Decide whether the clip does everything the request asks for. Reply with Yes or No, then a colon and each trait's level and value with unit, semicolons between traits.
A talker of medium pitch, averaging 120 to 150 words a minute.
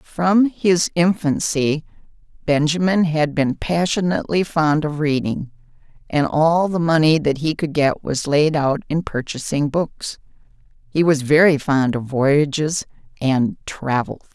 Yes: medium, 155 Hz; slow, 135 wpm